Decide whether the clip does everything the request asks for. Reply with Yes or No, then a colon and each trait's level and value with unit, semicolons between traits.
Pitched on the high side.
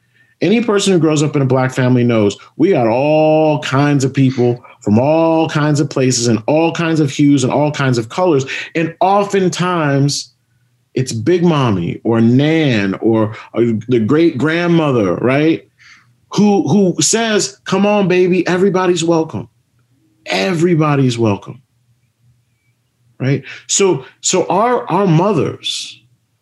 No: medium, 140 Hz